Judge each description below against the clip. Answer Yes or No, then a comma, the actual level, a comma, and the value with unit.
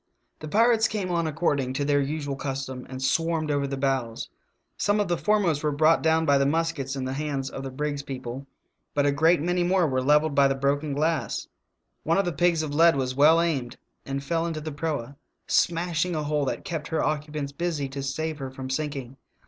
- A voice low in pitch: No, medium, 150 Hz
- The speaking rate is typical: No, fast, 215 wpm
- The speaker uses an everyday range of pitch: Yes, average, 3.1 semitones